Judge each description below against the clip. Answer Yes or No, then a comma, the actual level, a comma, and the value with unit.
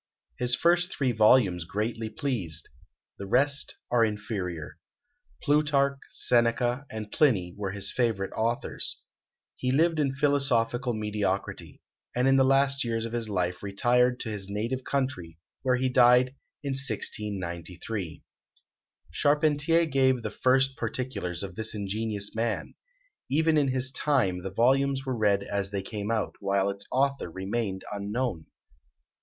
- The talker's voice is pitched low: Yes, low, 115 Hz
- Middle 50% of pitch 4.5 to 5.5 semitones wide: Yes, average, 5.0 semitones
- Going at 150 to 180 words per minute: No, average, 140 wpm